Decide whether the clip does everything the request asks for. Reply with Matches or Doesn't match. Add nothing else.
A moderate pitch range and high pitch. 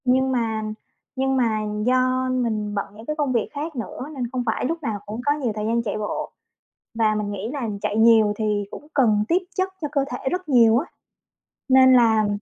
Matches